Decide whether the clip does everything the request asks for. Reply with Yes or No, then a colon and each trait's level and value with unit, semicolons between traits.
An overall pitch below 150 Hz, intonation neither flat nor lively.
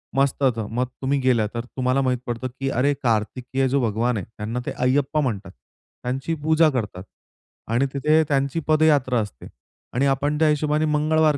Yes: low, 135 Hz; average, 3.4 semitones